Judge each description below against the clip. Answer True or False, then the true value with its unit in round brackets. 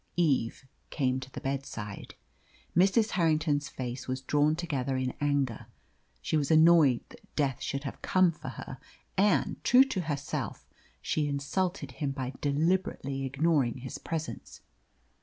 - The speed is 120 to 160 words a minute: True (140 wpm)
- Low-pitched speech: False (145 Hz)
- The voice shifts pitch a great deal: False (3.7 semitones)